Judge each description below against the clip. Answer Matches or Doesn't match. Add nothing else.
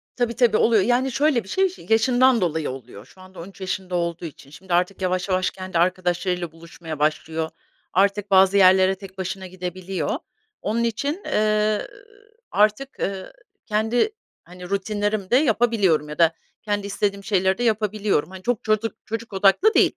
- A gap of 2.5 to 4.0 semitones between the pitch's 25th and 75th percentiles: Matches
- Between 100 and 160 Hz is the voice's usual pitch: Doesn't match